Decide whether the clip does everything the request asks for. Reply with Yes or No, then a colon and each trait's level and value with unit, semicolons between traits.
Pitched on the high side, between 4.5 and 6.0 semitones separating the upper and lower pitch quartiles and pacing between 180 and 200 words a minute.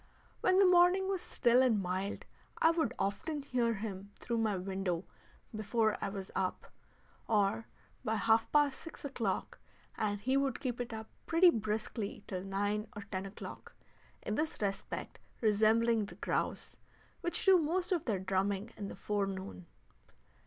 No: high, 220 Hz; average, 5.1 semitones; average, 155 wpm